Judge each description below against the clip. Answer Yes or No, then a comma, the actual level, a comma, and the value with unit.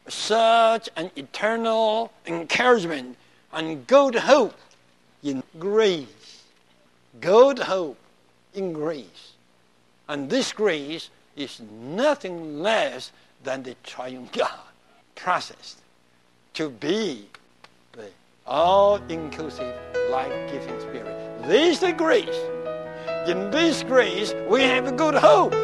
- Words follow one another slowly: Yes, slow, 95 wpm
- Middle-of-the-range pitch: Yes, medium, 160 Hz